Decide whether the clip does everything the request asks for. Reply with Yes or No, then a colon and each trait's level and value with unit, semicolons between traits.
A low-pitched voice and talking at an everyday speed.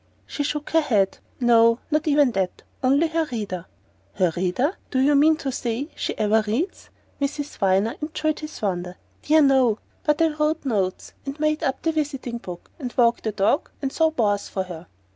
No: very high, 260 Hz; average, 185 wpm